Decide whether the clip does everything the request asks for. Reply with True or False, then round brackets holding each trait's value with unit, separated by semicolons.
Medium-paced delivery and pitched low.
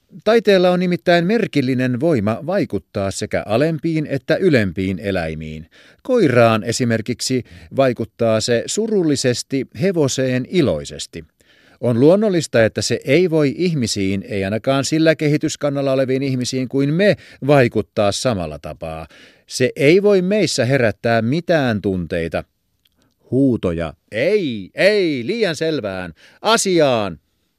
True (105 wpm; 125 Hz)